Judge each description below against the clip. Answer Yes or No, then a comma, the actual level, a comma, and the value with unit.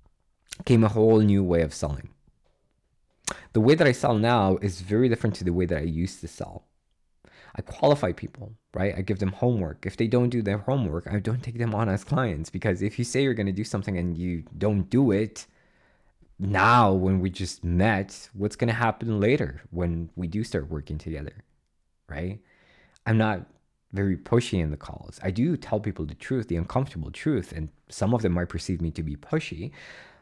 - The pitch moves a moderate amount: Yes, average, 4.9 semitones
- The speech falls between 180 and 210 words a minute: Yes, fast, 205 wpm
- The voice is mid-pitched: No, low, 100 Hz